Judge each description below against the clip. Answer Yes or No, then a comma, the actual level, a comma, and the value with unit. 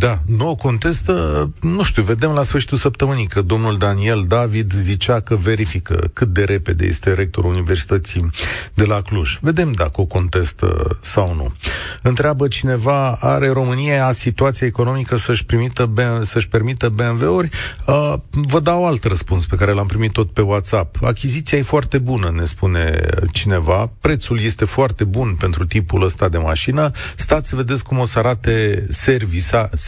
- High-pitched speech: No, low, 110 Hz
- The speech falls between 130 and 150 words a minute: No, average, 160 wpm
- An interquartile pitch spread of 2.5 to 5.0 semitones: No, wide, 5.6 semitones